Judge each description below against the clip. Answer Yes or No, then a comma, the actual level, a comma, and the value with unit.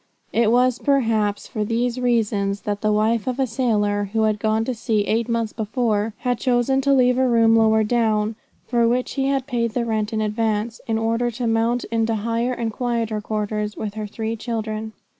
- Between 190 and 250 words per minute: Yes, average, 195 wpm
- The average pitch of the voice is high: Yes, high, 225 Hz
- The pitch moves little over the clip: Yes, narrow, 2.0 semitones